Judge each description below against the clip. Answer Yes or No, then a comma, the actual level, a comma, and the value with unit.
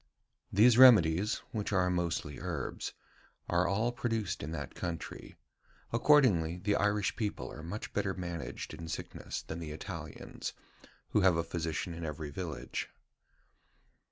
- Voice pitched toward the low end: Yes, very low, 90 Hz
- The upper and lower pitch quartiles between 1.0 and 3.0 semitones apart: No, average, 4.1 semitones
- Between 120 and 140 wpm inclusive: Yes, slow, 135 wpm